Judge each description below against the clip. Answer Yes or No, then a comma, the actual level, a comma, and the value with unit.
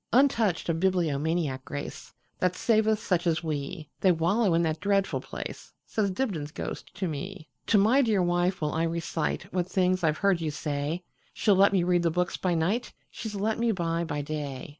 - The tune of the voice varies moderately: Yes, average, 3.7 semitones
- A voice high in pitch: No, medium, 175 Hz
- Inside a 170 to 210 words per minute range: Yes, average, 175 wpm